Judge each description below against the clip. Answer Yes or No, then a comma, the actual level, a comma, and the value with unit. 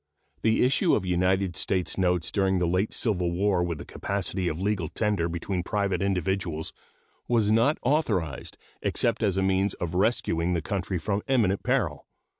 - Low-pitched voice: Yes, very low, 95 Hz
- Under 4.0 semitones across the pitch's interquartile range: Yes, average, 2.8 semitones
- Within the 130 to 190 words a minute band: Yes, average, 165 wpm